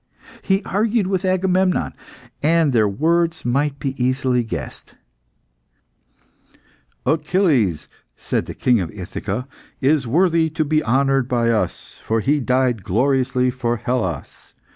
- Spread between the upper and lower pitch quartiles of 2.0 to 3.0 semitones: No, average, 5.2 semitones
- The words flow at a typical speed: No, slow, 120 wpm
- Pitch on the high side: No, low, 135 Hz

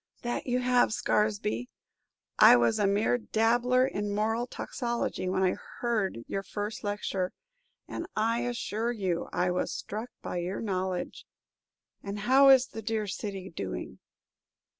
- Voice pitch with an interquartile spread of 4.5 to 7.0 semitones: No, average, 4.0 semitones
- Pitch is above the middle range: Yes, high, 210 Hz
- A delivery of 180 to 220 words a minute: No, average, 140 wpm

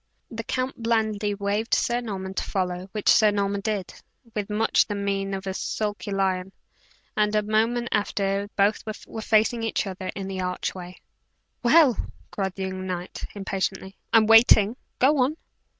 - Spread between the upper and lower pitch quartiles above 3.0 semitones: No, narrow, 2.5 semitones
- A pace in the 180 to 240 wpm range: No, average, 165 wpm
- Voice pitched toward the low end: No, high, 205 Hz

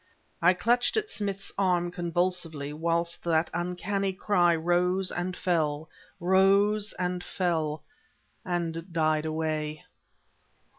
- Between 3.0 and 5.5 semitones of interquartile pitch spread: No, narrow, 2.6 semitones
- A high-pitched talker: No, medium, 175 Hz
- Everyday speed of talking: No, slow, 105 wpm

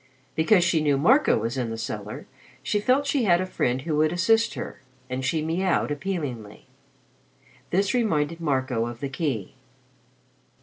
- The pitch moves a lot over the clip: Yes, wide, 6.3 semitones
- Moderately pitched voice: Yes, medium, 155 Hz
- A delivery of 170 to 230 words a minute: No, average, 160 wpm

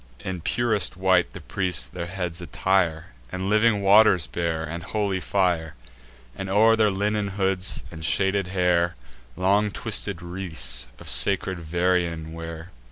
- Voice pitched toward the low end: Yes, very low, 95 Hz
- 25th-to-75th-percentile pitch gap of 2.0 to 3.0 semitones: Yes, average, 2.7 semitones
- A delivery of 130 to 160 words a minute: Yes, average, 140 wpm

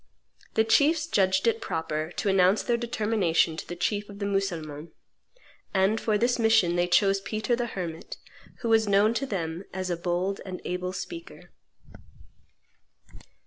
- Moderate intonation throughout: Yes, average, 4.0 semitones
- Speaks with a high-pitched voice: Yes, high, 195 Hz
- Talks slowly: No, average, 155 wpm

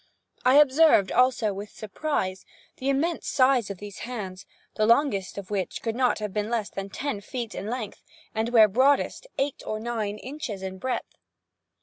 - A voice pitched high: Yes, high, 225 Hz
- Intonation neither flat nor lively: Yes, average, 4.3 semitones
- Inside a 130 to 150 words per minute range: No, average, 175 wpm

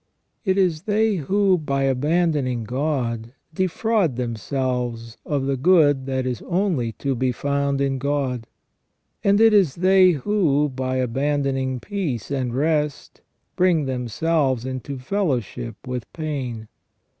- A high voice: No, medium, 140 Hz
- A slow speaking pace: Yes, slow, 125 wpm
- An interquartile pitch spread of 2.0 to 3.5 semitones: No, average, 4.7 semitones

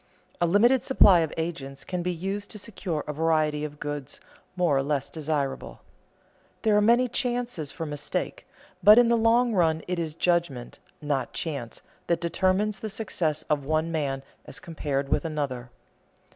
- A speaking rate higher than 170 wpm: No, average, 165 wpm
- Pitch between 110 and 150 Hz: No, medium, 165 Hz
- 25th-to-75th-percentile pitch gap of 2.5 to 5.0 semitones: No, wide, 5.5 semitones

